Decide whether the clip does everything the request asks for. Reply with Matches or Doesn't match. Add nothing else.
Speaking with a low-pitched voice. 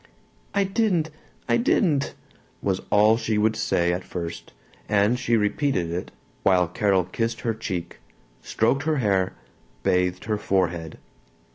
Matches